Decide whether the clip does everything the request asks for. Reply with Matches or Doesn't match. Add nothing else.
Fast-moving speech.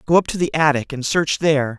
Matches